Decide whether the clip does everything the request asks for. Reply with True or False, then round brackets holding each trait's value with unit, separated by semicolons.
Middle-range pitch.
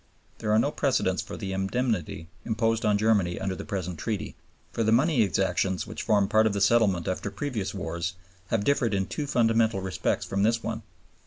False (105 Hz)